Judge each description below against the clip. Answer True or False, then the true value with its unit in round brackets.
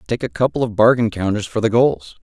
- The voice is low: True (110 Hz)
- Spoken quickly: True (240 wpm)